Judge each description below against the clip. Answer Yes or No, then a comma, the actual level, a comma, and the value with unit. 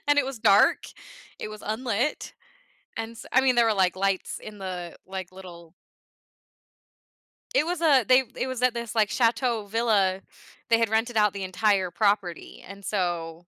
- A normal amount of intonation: Yes, average, 3.9 semitones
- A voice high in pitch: Yes, high, 215 Hz